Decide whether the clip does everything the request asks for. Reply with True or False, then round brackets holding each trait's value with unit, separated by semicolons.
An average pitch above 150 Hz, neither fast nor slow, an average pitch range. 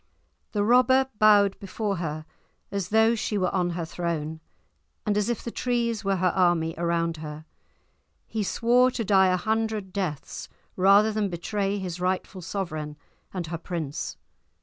True (190 Hz; 155 wpm; 3.9 semitones)